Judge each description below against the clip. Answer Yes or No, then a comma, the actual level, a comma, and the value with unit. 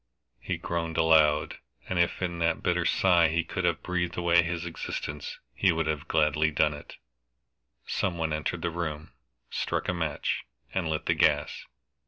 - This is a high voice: No, very low, 80 Hz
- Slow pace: No, average, 170 wpm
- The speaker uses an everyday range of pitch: No, narrow, 1.9 semitones